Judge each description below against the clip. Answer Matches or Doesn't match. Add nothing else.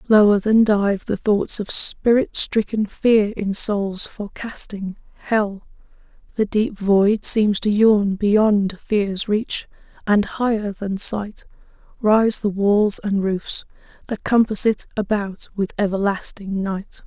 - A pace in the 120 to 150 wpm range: Matches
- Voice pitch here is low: Doesn't match